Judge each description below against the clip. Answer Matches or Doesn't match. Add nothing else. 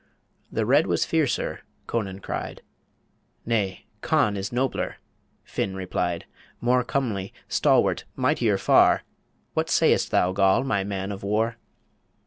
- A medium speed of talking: Doesn't match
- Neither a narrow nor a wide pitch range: Matches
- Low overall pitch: Matches